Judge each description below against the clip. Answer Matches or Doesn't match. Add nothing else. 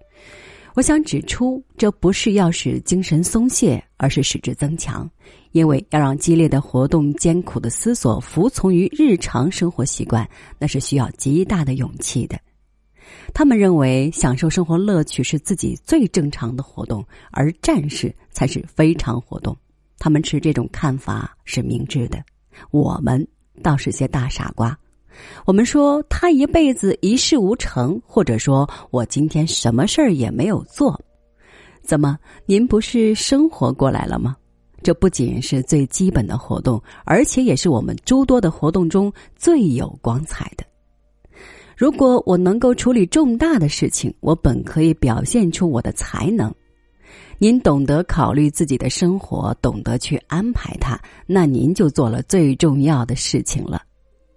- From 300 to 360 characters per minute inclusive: Doesn't match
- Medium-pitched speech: Matches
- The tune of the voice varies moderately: Doesn't match